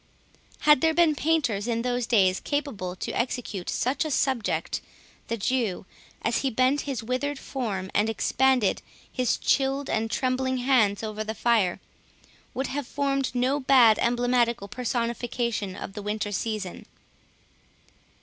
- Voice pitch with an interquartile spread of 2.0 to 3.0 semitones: No, average, 3.6 semitones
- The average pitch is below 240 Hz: No, high, 245 Hz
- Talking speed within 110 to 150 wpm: Yes, average, 140 wpm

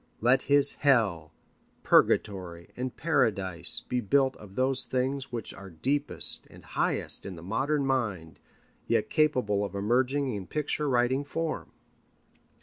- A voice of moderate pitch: No, low, 125 Hz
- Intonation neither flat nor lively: No, wide, 5.9 semitones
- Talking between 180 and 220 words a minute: No, slow, 135 wpm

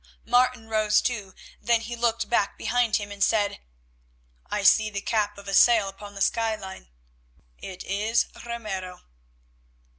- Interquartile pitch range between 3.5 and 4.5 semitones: No, narrow, 2.5 semitones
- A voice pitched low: No, high, 215 Hz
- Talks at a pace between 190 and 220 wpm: No, average, 145 wpm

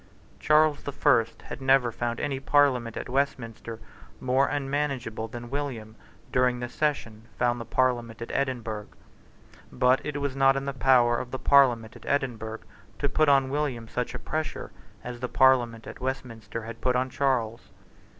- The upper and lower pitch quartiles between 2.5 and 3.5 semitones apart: Yes, average, 2.9 semitones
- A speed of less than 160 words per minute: No, average, 165 wpm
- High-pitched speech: No, low, 125 Hz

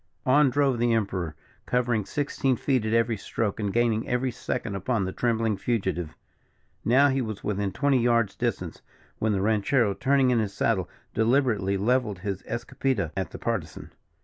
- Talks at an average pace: Yes, average, 165 wpm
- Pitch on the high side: No, low, 115 Hz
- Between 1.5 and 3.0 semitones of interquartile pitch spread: No, average, 3.9 semitones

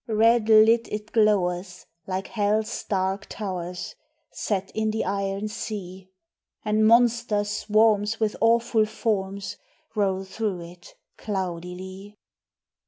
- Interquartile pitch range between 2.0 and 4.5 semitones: Yes, narrow, 2.4 semitones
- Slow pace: Yes, slow, 105 wpm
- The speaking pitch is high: Yes, high, 205 Hz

